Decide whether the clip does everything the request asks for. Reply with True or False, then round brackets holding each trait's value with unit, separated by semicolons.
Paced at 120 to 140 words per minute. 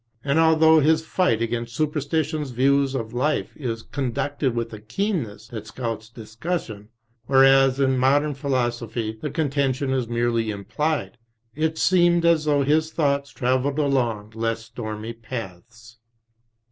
True (135 wpm)